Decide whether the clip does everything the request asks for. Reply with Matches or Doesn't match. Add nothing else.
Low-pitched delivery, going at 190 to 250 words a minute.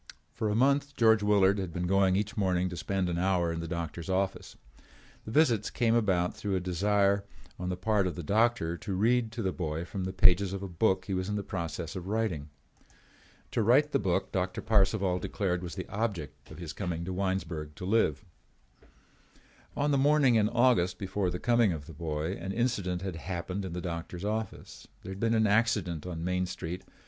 Matches